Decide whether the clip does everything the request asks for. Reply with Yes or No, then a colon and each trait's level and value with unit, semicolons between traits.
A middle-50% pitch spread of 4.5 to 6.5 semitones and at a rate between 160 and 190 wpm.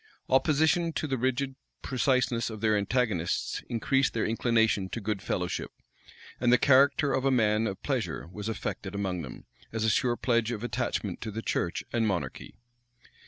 No: average, 3.7 semitones; average, 170 wpm